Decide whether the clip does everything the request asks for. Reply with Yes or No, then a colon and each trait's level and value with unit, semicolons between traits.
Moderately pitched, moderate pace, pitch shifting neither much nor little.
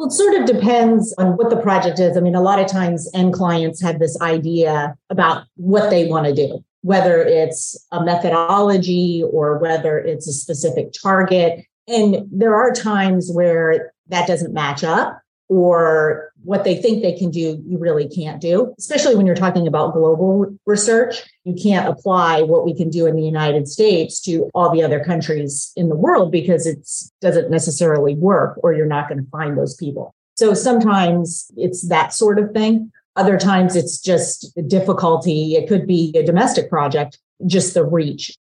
Yes: medium, 175 Hz; average, 185 wpm; average, 3.0 semitones